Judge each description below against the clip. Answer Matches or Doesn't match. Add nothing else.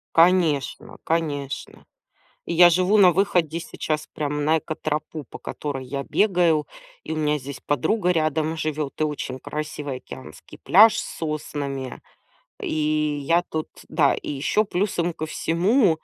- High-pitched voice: Doesn't match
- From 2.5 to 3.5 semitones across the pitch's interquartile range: Matches